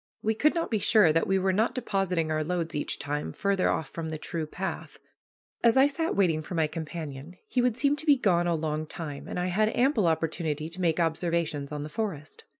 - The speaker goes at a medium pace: No, fast, 225 wpm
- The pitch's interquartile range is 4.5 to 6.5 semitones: Yes, average, 5.2 semitones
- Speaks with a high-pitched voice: No, medium, 170 Hz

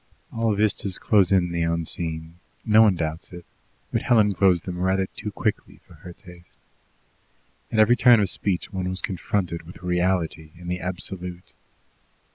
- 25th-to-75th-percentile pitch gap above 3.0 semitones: No, average, 2.7 semitones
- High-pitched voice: No, very low, 90 Hz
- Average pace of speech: Yes, average, 160 wpm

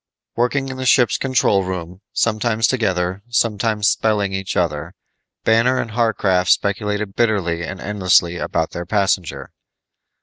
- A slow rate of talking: Yes, slow, 130 wpm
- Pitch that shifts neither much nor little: Yes, average, 3.8 semitones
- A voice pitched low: Yes, low, 100 Hz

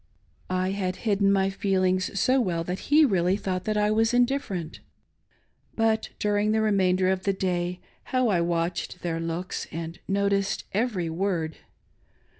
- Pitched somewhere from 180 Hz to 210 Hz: Yes, high, 190 Hz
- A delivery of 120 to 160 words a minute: Yes, average, 155 wpm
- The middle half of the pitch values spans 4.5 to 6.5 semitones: No, average, 2.7 semitones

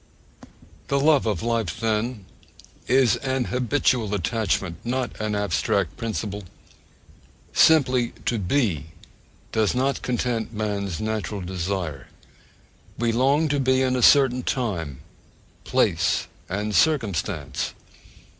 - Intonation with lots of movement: No, average, 4.2 semitones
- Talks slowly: Yes, slow, 110 wpm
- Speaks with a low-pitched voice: Yes, low, 115 Hz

